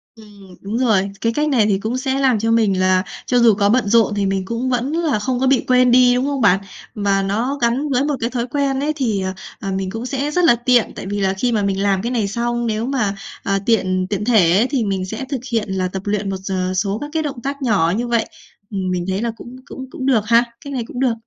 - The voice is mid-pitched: No, high, 230 Hz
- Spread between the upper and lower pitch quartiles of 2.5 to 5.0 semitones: Yes, average, 4.4 semitones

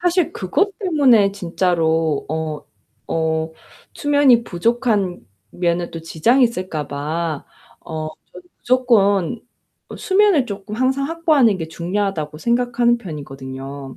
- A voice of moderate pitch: No, high, 195 Hz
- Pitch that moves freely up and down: Yes, wide, 7.5 semitones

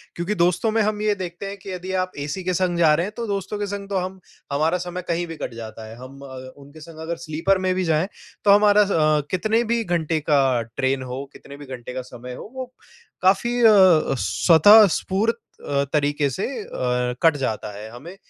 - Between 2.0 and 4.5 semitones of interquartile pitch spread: No, wide, 5.5 semitones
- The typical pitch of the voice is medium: Yes, medium, 175 Hz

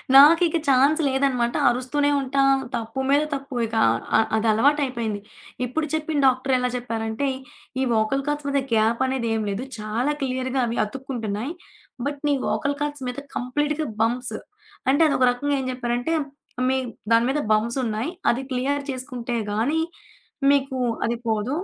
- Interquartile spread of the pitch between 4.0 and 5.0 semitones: No, average, 3.2 semitones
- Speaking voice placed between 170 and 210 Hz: No, very high, 255 Hz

